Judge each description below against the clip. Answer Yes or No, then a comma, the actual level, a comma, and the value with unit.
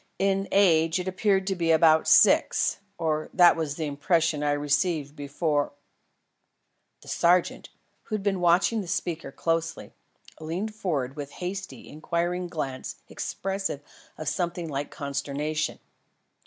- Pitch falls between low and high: Yes, medium, 165 Hz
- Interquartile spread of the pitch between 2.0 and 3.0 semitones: No, average, 3.7 semitones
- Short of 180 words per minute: Yes, average, 140 wpm